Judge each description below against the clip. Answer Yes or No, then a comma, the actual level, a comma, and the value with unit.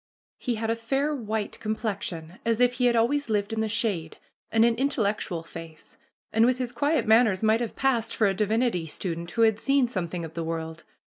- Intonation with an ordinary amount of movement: Yes, average, 4.4 semitones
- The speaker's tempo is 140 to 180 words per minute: No, fast, 205 wpm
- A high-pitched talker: Yes, high, 220 Hz